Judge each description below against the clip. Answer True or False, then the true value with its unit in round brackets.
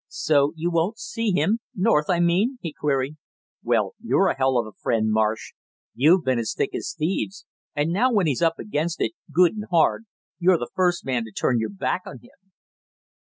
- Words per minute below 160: False (200 wpm)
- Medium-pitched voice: True (165 Hz)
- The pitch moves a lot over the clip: True (6.1 semitones)